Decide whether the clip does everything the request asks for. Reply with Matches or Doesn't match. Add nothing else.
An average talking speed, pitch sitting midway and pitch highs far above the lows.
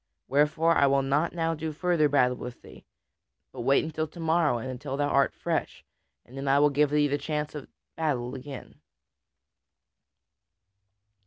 Doesn't match